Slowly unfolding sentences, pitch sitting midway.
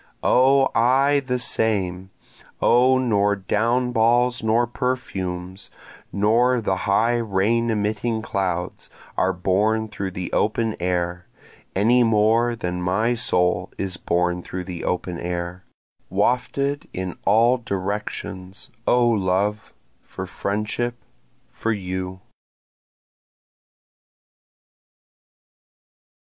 No: slow, 100 wpm; low, 105 Hz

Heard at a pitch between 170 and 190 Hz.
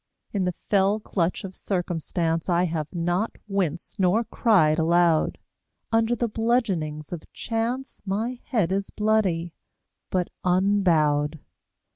Yes: medium, 185 Hz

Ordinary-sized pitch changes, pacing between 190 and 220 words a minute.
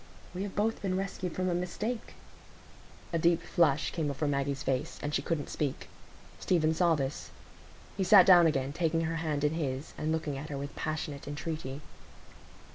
No: average, 3.5 semitones; average, 180 wpm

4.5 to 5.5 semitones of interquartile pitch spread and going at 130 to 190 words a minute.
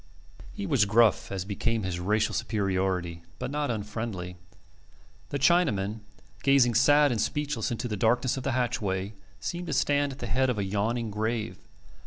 Yes: average, 4.9 semitones; average, 165 wpm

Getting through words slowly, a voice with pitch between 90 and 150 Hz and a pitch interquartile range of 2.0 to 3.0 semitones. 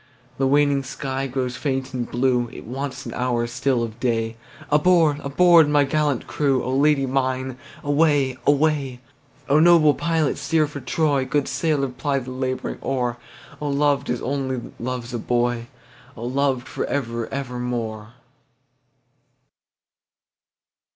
Yes: slow, 115 wpm; low, 135 Hz; average, 2.7 semitones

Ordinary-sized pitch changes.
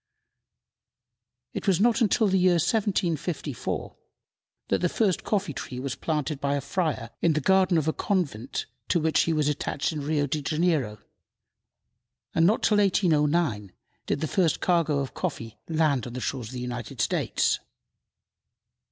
Yes: average, 4.6 semitones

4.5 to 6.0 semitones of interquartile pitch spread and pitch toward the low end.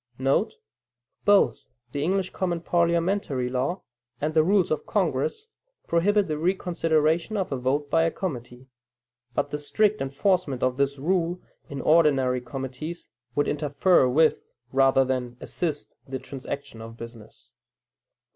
No: average, 4.8 semitones; medium, 150 Hz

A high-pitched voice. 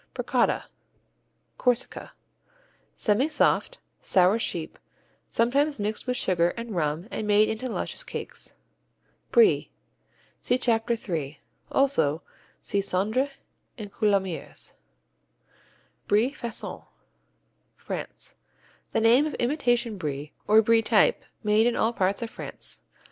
Yes: high, 220 Hz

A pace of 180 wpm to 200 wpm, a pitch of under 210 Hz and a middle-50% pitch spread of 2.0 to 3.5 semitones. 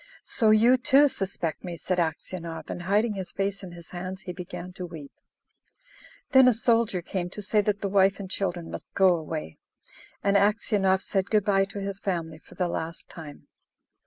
Yes: average, 190 wpm; high, 190 Hz; average, 2.8 semitones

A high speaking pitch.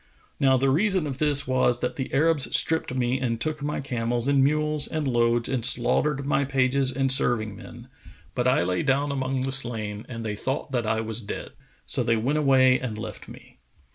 No: low, 130 Hz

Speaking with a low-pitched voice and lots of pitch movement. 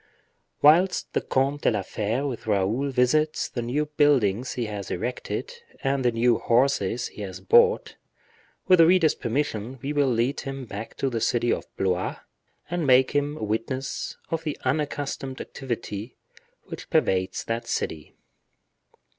No: low, 130 Hz; average, 4.3 semitones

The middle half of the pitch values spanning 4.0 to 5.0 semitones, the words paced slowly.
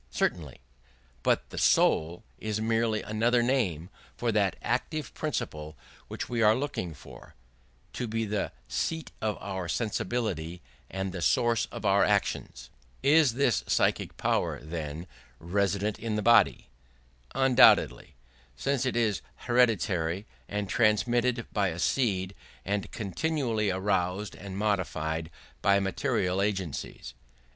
Yes: average, 4.4 semitones; slow, 125 wpm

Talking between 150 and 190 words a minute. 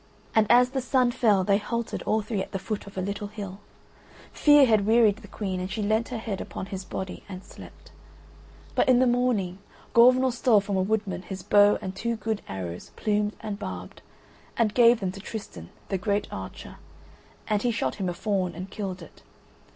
No: fast, 205 wpm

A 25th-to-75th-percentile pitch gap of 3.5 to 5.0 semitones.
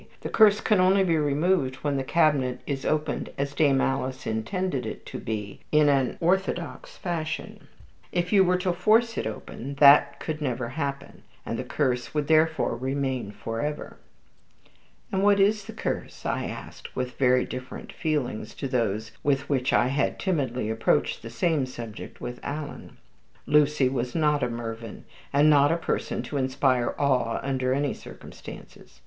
Yes: average, 3.9 semitones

